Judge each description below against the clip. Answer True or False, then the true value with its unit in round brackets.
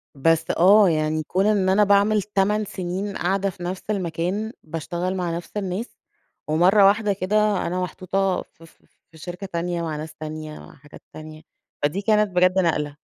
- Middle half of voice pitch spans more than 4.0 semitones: False (3.4 semitones)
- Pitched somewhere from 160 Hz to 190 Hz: True (185 Hz)